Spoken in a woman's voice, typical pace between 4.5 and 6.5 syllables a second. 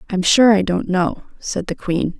No: female; 4.2 syllables/s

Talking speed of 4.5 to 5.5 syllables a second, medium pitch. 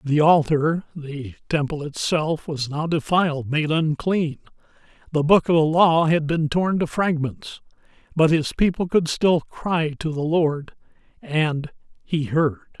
No: 4.0 syllables/s; medium, 155 Hz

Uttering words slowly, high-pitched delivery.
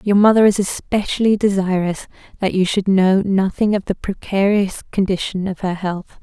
No: average, 165 wpm; high, 195 Hz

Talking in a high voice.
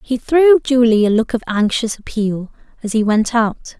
Yes: high, 230 Hz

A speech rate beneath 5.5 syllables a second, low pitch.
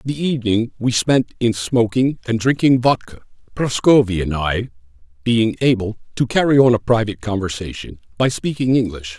Yes: 5.1 syllables/s; low, 115 Hz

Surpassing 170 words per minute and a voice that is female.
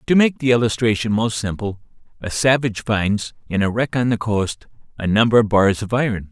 No: average, 200 wpm; male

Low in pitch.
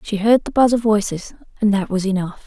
No: high, 205 Hz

